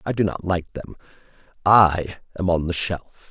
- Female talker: No, male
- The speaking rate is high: No, average, 180 wpm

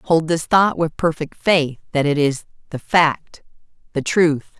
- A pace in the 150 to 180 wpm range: Yes, average, 170 wpm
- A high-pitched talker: No, medium, 155 Hz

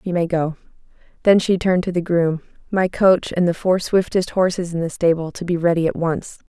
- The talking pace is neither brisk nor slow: No, fast, 220 wpm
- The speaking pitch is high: No, medium, 175 Hz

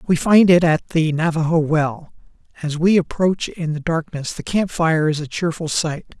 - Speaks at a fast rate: No, average, 195 wpm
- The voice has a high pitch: No, medium, 160 Hz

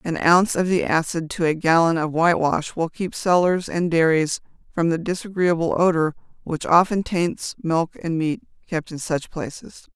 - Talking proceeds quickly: No, average, 175 wpm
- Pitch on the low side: No, medium, 170 Hz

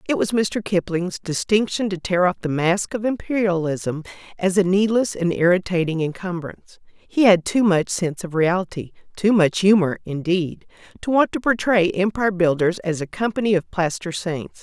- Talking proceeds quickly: No, average, 160 wpm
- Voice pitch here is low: No, medium, 185 Hz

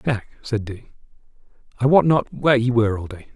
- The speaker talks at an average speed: Yes, average, 195 wpm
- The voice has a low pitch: Yes, low, 120 Hz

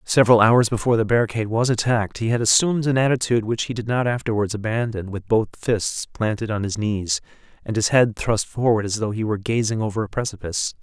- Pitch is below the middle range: Yes, low, 110 Hz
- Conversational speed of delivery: No, fast, 210 wpm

